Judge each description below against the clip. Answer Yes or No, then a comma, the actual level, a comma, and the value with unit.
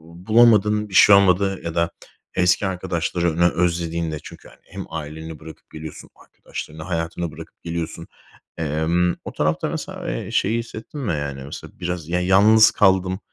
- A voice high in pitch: No, very low, 85 Hz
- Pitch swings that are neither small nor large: Yes, average, 3.0 semitones